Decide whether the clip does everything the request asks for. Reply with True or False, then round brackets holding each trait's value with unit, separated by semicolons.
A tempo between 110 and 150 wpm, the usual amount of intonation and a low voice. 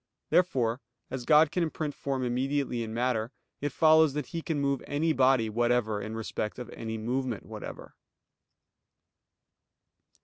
True (140 wpm; 3.9 semitones; 130 Hz)